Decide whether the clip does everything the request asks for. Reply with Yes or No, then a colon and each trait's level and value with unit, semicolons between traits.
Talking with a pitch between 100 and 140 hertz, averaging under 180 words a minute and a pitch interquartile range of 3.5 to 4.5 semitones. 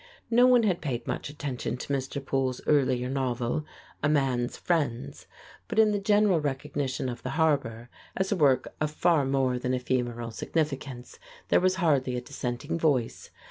Yes: low, 135 Hz; average, 165 wpm; average, 4.1 semitones